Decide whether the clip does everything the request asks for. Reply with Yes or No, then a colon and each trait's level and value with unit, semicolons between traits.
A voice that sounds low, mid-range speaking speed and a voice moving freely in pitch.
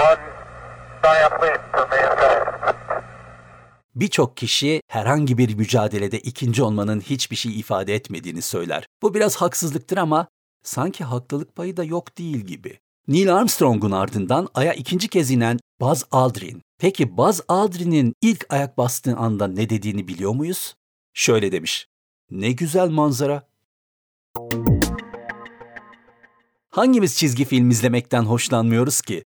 Yes: low, 125 Hz; average, 110 wpm; wide, 6.9 semitones